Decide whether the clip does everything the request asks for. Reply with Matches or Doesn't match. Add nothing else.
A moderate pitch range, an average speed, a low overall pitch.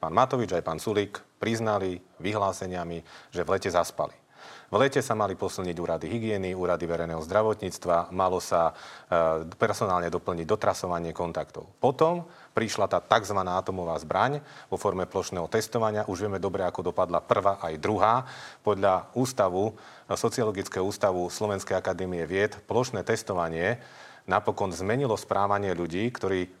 Matches